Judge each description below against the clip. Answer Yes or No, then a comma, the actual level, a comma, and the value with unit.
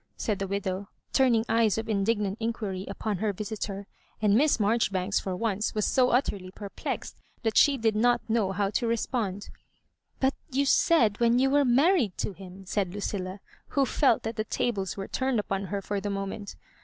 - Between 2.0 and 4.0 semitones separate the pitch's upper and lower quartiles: Yes, average, 3.1 semitones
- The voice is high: Yes, high, 210 Hz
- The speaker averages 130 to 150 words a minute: No, average, 185 wpm